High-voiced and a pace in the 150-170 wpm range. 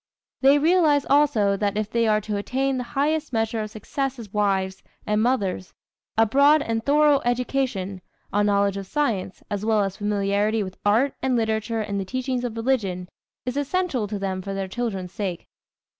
No: high, 220 Hz; average, 180 wpm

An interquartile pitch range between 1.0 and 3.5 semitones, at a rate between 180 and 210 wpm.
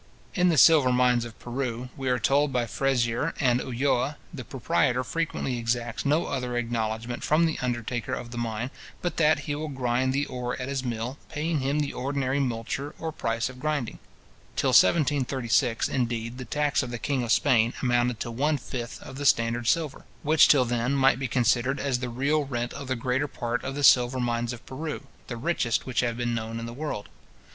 Yes: average, 2.8 semitones; average, 200 wpm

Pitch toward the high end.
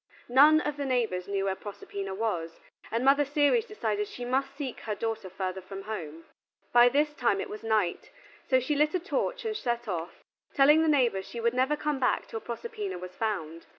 Yes: high, 240 Hz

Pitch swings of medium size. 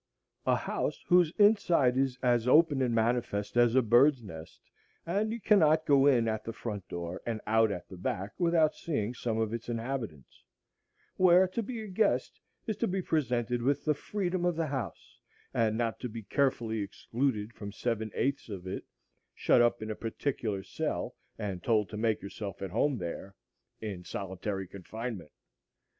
No: wide, 5.8 semitones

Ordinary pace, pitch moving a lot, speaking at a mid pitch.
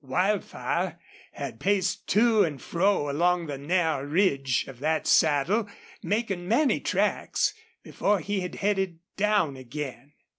No: slow, 125 wpm; wide, 6.0 semitones; medium, 175 Hz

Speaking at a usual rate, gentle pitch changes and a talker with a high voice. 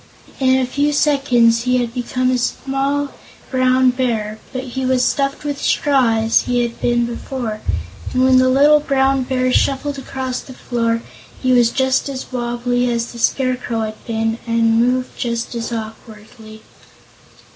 Yes: average, 160 wpm; narrow, 2.1 semitones; very high, 250 Hz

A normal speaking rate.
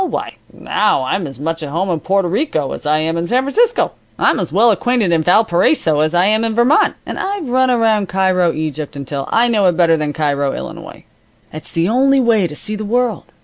No: fast, 220 wpm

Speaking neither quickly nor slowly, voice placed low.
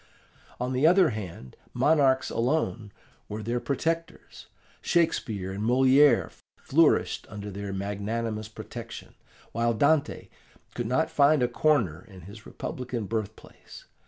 No: slow, 120 wpm; low, 115 Hz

